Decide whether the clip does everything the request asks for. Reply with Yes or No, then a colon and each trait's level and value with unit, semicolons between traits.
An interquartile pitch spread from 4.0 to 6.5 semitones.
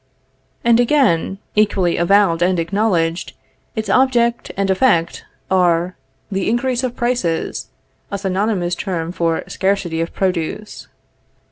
Yes: average, 4.5 semitones